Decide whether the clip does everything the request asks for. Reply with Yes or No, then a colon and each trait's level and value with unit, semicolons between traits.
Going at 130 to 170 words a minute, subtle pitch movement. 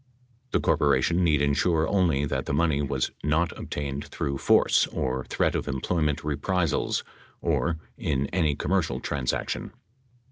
No: average, 140 wpm; average, 3.3 semitones